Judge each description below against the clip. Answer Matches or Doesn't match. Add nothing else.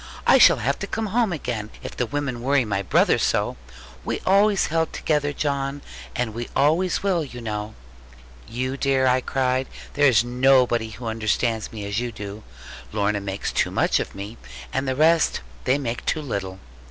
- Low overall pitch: Matches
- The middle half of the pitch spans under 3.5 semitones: Doesn't match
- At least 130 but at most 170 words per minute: Doesn't match